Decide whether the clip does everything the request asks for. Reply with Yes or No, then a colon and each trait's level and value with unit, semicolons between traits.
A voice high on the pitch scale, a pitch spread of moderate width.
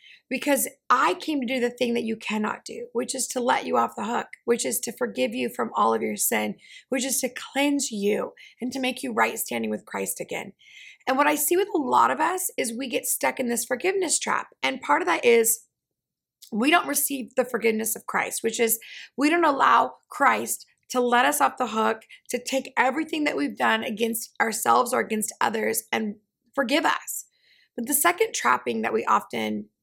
Yes: very high, 255 Hz; average, 4.0 semitones